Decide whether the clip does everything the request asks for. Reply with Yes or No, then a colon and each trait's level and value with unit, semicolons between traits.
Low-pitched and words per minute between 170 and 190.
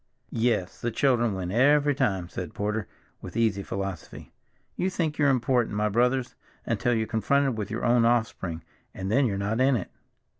Yes: low, 115 Hz; average, 175 wpm